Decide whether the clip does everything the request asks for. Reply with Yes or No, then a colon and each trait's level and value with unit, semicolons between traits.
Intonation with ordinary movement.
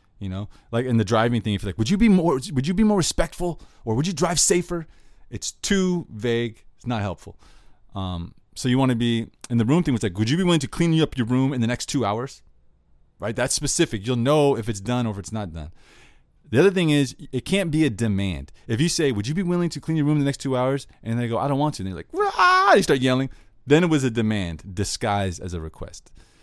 No: wide, 6.2 semitones